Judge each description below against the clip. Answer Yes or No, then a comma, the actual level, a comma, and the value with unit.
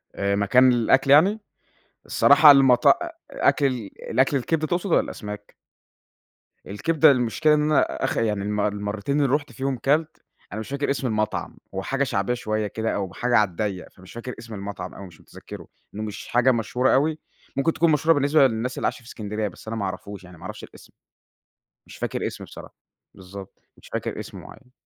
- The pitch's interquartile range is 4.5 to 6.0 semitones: Yes, average, 5.2 semitones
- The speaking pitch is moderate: No, low, 120 Hz